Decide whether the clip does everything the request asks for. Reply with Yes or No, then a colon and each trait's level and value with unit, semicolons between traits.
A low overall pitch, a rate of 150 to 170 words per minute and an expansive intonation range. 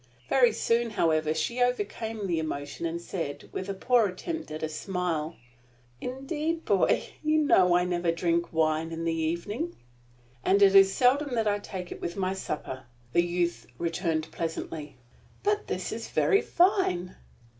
No: medium, 180 Hz; average, 160 wpm; wide, 6.3 semitones